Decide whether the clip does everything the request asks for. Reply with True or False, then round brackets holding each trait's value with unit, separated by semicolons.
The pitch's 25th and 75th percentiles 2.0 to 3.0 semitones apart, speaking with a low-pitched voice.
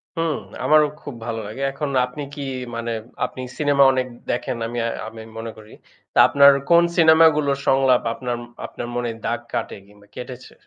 False (3.8 semitones; 130 Hz)